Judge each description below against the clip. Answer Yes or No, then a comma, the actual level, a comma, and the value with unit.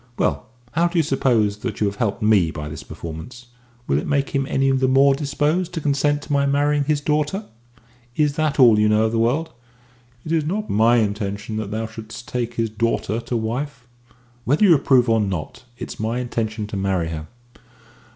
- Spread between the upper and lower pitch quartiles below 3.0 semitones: No, average, 5.2 semitones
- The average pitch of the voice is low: Yes, low, 120 Hz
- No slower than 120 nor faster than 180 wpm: No, average, 200 wpm